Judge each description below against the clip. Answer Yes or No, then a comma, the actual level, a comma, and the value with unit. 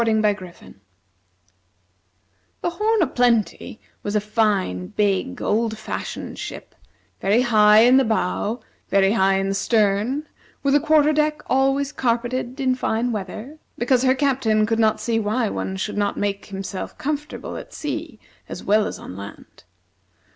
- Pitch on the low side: No, high, 225 Hz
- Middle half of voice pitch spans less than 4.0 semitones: No, average, 4.5 semitones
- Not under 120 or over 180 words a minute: Yes, average, 145 wpm